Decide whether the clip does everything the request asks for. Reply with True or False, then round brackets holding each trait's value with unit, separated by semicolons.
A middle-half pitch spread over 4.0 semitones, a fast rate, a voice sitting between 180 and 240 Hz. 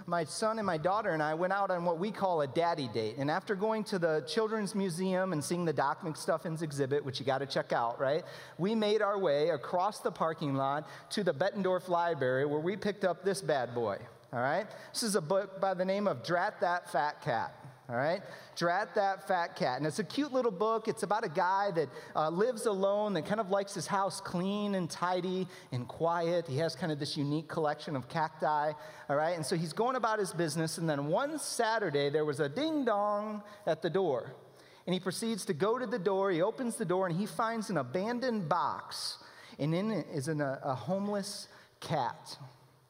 True (4.9 semitones; 220 wpm; 185 Hz)